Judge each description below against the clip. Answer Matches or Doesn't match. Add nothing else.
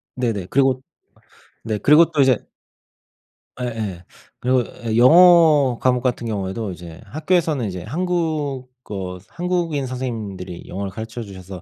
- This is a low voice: Matches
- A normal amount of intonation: Doesn't match